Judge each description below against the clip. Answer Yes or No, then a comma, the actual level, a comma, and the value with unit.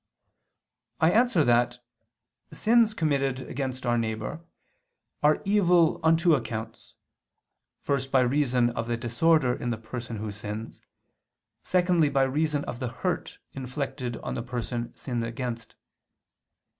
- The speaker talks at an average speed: No, slow, 130 wpm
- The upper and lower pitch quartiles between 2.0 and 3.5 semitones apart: No, average, 4.5 semitones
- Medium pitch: No, low, 130 Hz